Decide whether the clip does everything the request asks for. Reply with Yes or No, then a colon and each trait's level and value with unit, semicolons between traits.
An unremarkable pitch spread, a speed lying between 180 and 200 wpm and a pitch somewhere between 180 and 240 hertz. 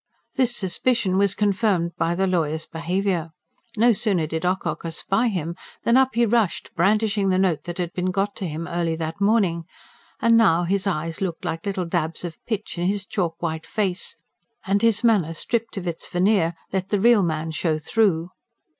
Yes: average, 3.8 semitones; average, 185 wpm; medium, 185 Hz